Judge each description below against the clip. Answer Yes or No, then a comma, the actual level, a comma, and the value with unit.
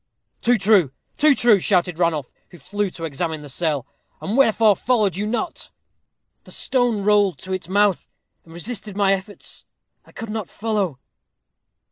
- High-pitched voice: Yes, high, 200 Hz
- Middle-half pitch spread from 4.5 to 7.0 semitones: No, average, 4.0 semitones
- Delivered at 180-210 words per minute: No, average, 155 wpm